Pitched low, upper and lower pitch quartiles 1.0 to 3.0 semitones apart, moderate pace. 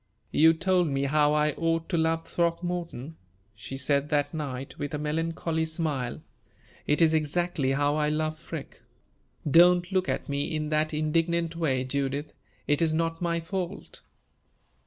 No: medium, 155 Hz; narrow, 2.4 semitones; average, 155 wpm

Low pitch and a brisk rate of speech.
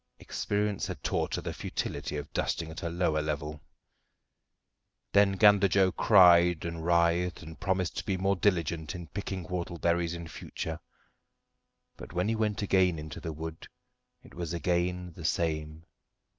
No: very low, 85 Hz; average, 155 wpm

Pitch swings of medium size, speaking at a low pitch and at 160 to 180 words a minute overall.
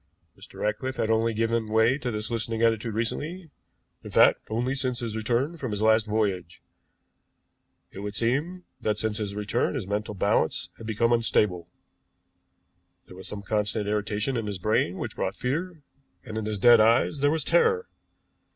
Yes: average, 3.1 semitones; low, 110 Hz; average, 170 wpm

